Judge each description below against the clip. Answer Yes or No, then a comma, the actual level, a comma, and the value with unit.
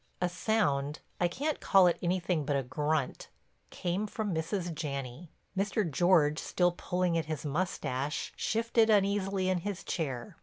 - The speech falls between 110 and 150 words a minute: Yes, average, 140 wpm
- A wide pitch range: No, average, 4.4 semitones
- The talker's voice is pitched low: No, medium, 175 Hz